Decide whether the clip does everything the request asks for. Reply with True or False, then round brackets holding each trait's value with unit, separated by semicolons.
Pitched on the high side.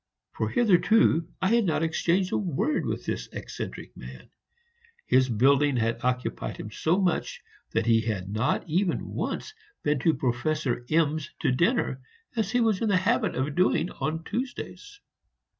False (160 Hz)